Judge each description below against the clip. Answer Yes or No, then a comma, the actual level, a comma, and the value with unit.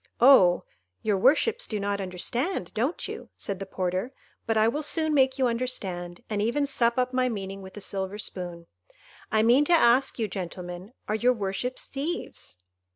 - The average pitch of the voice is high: Yes, high, 220 Hz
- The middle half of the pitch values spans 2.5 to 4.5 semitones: No, average, 5.2 semitones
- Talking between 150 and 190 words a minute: Yes, average, 175 wpm